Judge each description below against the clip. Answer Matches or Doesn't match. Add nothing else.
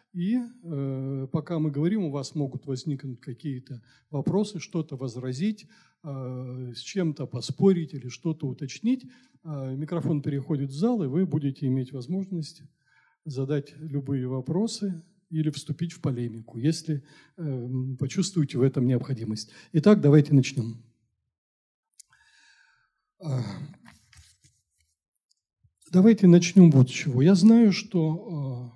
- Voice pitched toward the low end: Doesn't match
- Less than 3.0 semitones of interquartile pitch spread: Doesn't match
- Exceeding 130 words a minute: Doesn't match